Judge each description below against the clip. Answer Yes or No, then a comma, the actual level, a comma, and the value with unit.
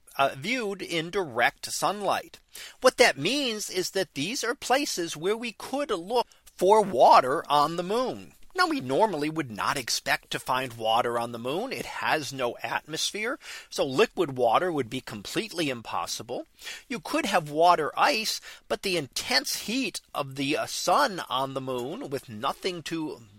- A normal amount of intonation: No, wide, 7.4 semitones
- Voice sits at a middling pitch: Yes, medium, 160 Hz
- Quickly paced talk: No, average, 165 wpm